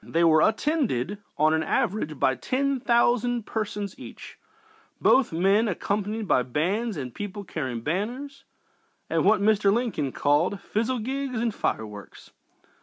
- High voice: Yes, high, 205 Hz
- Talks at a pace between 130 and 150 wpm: Yes, slow, 135 wpm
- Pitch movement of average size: No, wide, 7.0 semitones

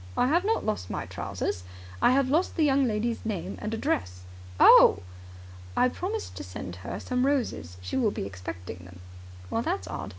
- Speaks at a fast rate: No, average, 175 wpm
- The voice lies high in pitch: Yes, high, 215 Hz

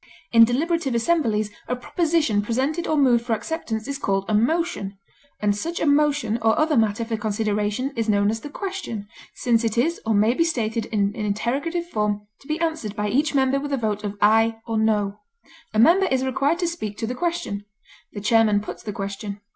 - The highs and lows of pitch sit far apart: Yes, wide, 5.7 semitones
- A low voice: No, high, 230 Hz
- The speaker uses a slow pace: No, average, 200 wpm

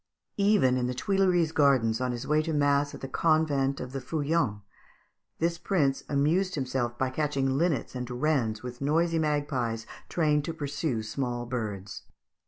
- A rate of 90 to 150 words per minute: No, average, 160 wpm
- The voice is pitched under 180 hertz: Yes, medium, 140 Hz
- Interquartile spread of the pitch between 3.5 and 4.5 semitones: Yes, average, 3.9 semitones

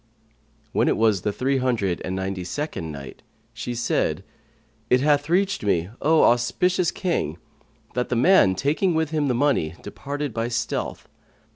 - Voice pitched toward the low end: Yes, low, 125 Hz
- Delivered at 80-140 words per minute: No, average, 155 wpm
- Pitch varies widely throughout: Yes, wide, 7.6 semitones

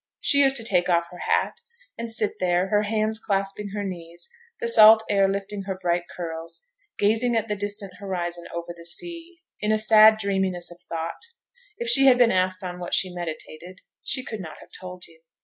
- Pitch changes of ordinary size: Yes, average, 3.7 semitones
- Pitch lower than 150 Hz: No, high, 195 Hz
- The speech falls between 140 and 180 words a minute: No, average, 200 wpm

